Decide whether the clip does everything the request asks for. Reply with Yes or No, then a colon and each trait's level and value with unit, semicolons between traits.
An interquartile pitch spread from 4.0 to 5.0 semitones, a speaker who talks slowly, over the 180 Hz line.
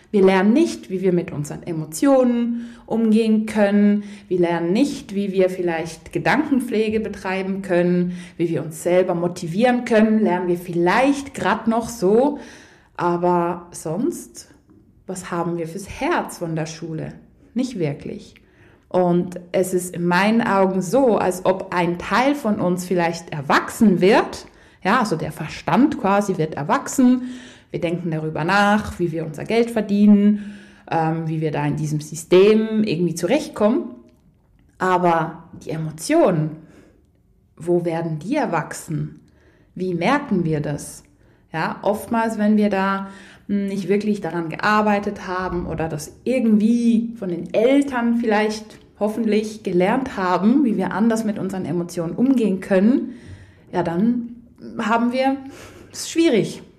No: average, 4.5 semitones; average, 135 wpm; high, 190 Hz